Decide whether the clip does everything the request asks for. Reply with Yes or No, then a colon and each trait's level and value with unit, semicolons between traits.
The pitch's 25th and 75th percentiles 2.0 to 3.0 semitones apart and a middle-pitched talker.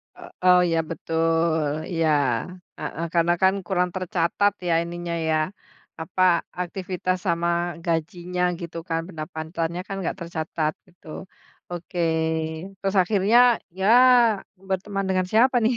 Yes: narrow, 2.4 semitones; medium, 175 Hz